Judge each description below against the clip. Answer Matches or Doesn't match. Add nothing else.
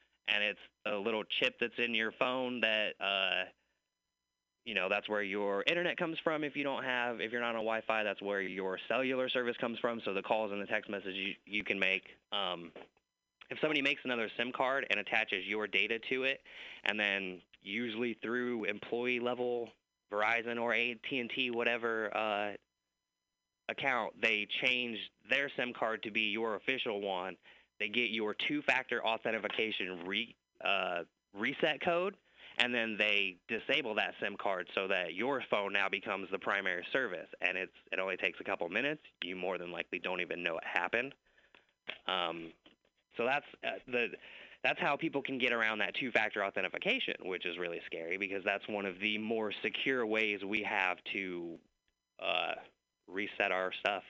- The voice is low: Matches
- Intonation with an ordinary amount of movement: Matches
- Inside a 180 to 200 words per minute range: Doesn't match